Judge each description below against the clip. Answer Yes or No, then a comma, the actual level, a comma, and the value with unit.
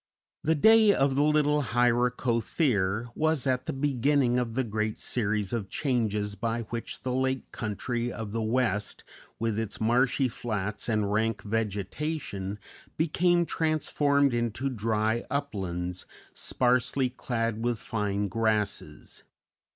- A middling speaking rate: No, slow, 125 wpm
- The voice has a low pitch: Yes, low, 120 Hz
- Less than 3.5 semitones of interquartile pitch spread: No, average, 3.9 semitones